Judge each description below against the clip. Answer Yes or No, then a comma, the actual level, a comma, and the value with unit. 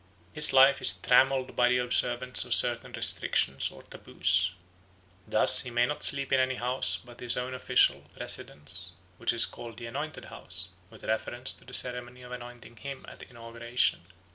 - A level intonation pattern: Yes, narrow, 1.8 semitones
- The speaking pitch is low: Yes, low, 125 Hz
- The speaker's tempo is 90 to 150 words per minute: No, average, 170 wpm